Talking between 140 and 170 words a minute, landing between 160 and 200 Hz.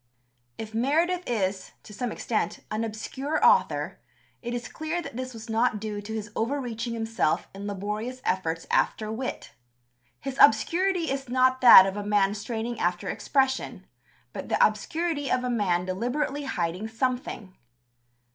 No: average, 155 wpm; high, 230 Hz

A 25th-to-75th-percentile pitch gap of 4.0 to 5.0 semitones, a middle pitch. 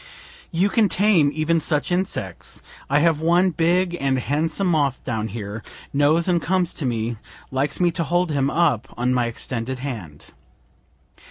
No: wide, 5.5 semitones; medium, 150 Hz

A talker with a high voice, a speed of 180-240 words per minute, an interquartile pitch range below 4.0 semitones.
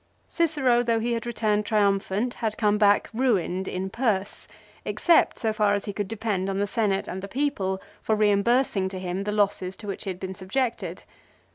Yes: high, 205 Hz; average, 190 wpm; average, 3.1 semitones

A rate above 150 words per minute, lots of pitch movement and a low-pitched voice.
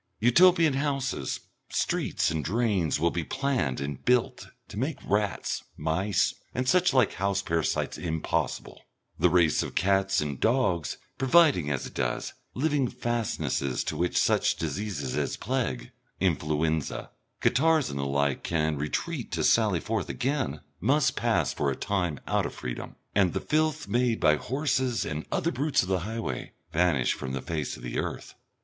Yes: average, 160 wpm; wide, 8.7 semitones; very low, 95 Hz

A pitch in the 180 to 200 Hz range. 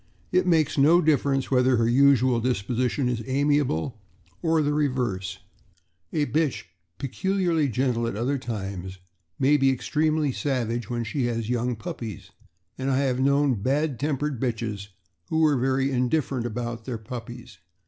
No: low, 130 Hz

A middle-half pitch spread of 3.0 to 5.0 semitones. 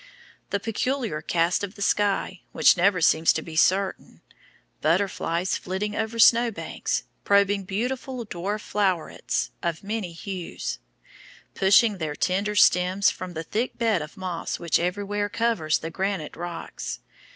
Yes: average, 3.4 semitones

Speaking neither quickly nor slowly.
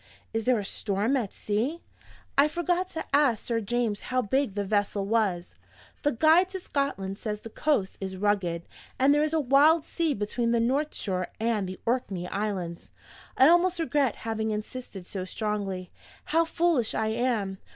Yes: average, 170 wpm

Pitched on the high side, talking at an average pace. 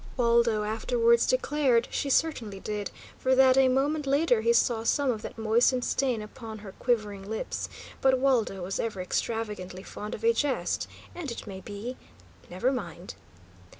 Yes: high, 235 Hz; average, 160 wpm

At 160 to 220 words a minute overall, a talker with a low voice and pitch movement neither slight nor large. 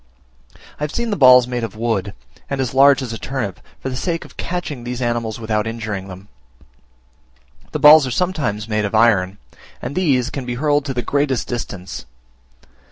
Yes: average, 185 wpm; low, 125 Hz; average, 4.3 semitones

